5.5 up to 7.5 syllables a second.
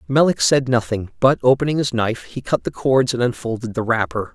Yes: 5.7 syllables/s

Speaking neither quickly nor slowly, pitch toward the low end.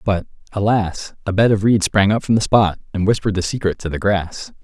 No: fast, 235 wpm; low, 100 Hz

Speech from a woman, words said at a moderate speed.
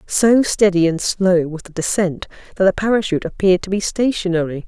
Yes: female; average, 180 wpm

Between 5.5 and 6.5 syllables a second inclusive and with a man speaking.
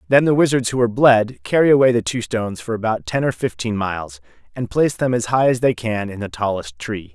Yes: 5.9 syllables/s; male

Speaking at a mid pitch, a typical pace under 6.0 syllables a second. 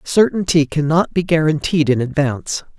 Yes: medium, 155 Hz; 5.0 syllables/s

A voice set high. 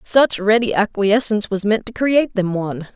Yes: high, 215 Hz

